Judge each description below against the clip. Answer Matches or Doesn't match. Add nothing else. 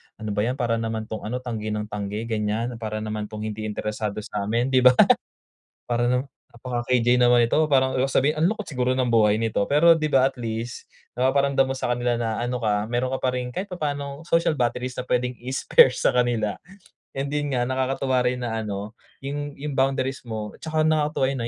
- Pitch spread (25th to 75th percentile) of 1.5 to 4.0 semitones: Matches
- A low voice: Matches